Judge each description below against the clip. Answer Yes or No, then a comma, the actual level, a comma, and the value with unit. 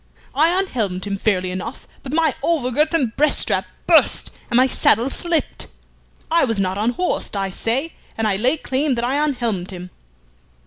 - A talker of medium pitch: No, high, 245 Hz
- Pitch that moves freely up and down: Yes, wide, 7.0 semitones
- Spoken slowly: No, average, 175 wpm